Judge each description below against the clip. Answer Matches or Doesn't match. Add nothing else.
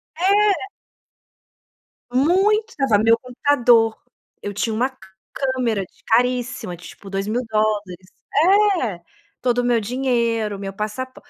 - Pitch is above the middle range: Matches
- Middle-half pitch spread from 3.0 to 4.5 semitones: Matches